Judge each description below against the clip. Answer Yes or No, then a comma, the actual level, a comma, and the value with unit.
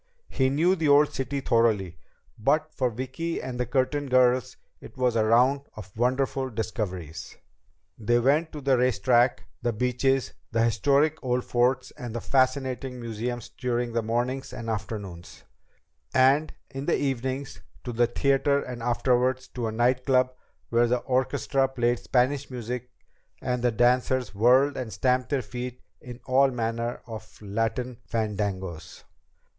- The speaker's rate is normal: Yes, average, 150 wpm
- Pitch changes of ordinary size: No, narrow, 2.2 semitones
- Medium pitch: No, low, 125 Hz